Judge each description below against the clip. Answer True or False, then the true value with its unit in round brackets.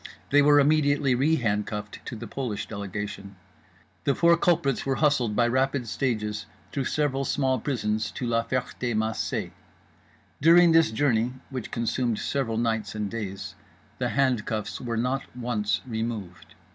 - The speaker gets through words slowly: False (145 wpm)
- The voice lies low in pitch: True (120 Hz)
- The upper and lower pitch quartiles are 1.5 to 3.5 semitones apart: False (4.1 semitones)